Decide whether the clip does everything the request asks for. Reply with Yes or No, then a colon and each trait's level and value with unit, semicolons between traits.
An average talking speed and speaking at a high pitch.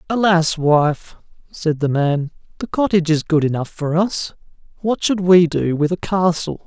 No: average, 170 wpm; medium, 170 Hz